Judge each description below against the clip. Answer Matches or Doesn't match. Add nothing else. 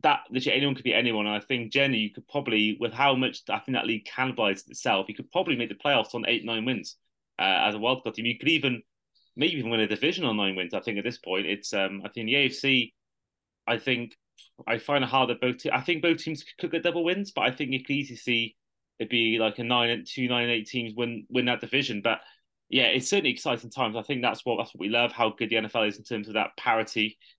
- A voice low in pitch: Matches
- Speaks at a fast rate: Matches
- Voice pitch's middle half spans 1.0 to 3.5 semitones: Matches